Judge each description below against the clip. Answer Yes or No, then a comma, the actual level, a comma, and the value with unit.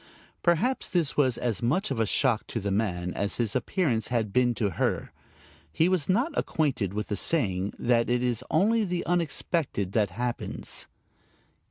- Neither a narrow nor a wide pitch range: No, wide, 7.7 semitones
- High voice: No, low, 125 Hz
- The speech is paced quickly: No, average, 170 wpm